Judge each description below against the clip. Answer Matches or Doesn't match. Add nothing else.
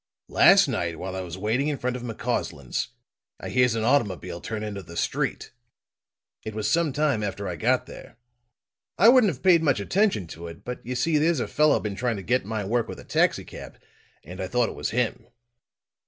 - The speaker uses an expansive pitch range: Matches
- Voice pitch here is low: Matches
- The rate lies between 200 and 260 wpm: Matches